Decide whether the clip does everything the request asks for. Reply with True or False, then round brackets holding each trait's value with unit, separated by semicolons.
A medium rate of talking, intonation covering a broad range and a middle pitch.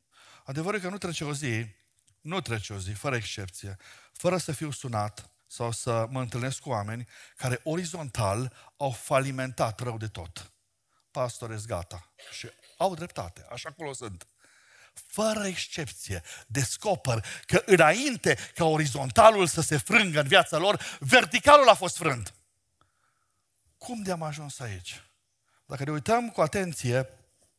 False (140 wpm; 6.6 semitones; 130 Hz)